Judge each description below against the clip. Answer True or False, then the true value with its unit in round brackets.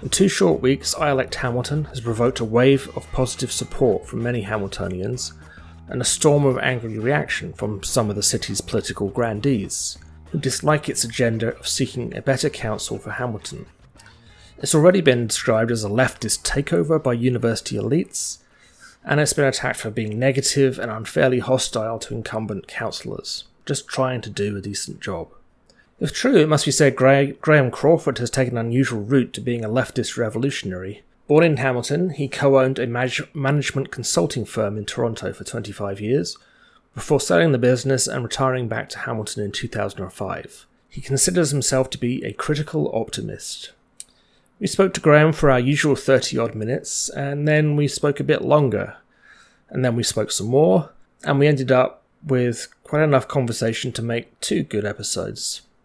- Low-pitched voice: True (130 Hz)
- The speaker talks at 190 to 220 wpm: False (175 wpm)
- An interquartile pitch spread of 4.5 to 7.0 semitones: False (4.0 semitones)